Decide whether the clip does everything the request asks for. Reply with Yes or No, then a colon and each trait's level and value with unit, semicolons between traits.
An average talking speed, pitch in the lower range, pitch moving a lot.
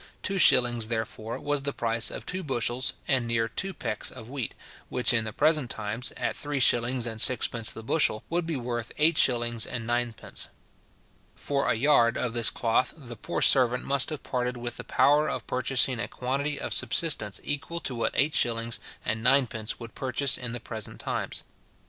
No: average, 185 wpm; low, 120 Hz; average, 3.2 semitones